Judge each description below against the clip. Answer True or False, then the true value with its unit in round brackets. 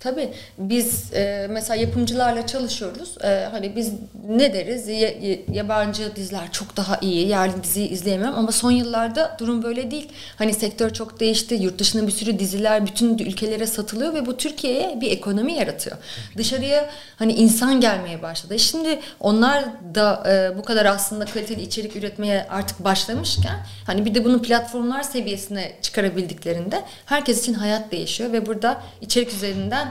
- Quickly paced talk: True (145 wpm)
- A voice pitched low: False (220 Hz)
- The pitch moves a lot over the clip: False (3.2 semitones)